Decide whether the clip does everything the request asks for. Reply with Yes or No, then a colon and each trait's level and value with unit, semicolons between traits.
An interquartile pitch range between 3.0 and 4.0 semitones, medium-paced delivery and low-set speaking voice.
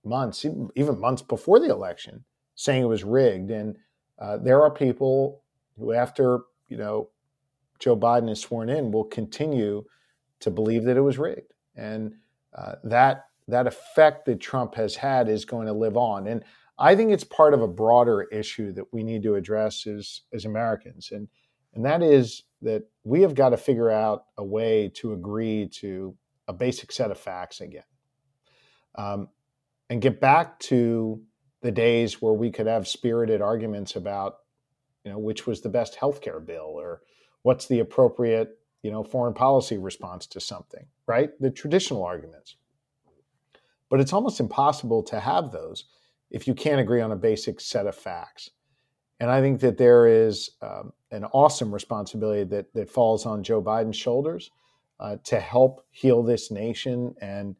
Yes: average, 3.7 semitones; average, 170 wpm; low, 120 Hz